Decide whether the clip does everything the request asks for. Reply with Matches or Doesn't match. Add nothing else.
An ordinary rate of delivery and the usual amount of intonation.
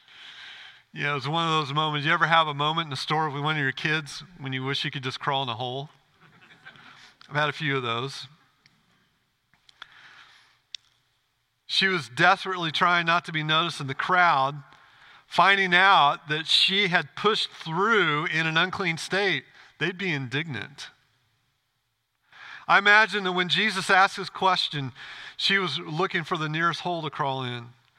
Matches